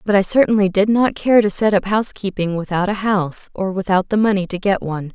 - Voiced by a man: No, female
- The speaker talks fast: Yes, fast, 235 wpm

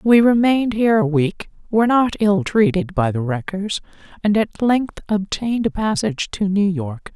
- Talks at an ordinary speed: Yes, average, 175 wpm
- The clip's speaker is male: No, female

